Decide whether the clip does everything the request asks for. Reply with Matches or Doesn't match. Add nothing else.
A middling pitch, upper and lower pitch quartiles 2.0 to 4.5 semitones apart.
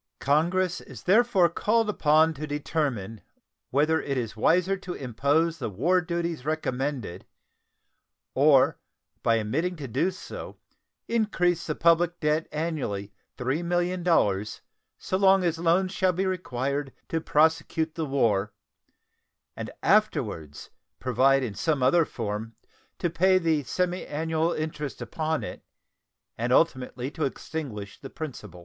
Doesn't match